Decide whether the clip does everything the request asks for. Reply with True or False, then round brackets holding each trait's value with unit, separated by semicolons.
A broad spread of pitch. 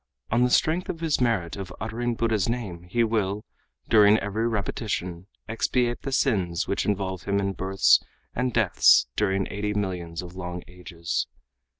False (4.1 semitones)